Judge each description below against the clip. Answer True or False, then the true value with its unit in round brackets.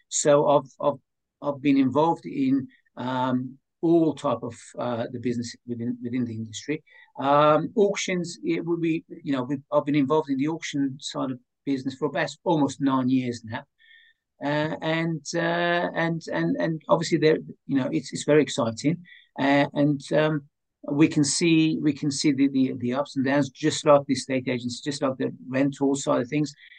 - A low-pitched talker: False (145 Hz)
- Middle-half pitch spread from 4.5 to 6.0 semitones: False (3.3 semitones)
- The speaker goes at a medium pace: True (180 wpm)